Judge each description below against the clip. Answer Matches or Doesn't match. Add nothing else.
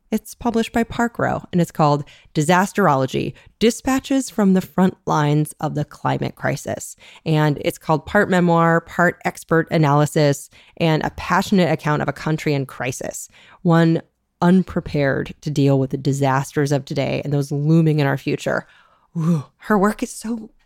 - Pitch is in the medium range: Matches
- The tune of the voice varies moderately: Matches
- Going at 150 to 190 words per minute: Matches